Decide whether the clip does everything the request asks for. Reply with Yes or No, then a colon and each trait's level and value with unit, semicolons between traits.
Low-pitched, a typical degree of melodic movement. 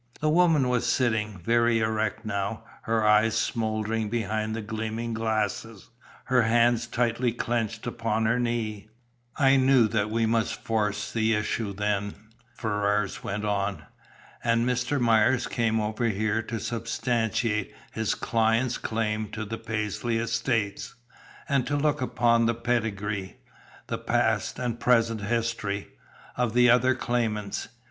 No: low, 115 Hz; narrow, 1.8 semitones